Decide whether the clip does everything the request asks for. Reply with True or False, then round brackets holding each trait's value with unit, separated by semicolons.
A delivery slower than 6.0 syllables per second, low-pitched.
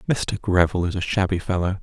False (6.3 syllables/s; 95 Hz)